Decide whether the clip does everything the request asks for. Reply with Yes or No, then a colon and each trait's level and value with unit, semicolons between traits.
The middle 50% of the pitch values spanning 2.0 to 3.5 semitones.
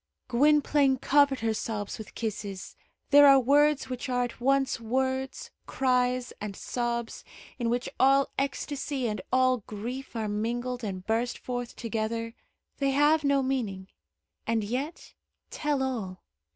Yes: average, 3.2 semitones